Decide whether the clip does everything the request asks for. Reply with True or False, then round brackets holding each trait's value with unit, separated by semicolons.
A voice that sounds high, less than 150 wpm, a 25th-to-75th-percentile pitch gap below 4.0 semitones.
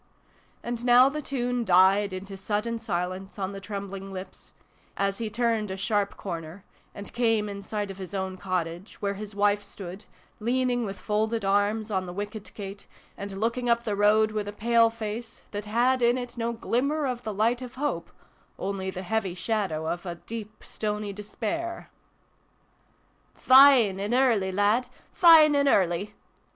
False (210 Hz; 170 wpm; 3.2 semitones)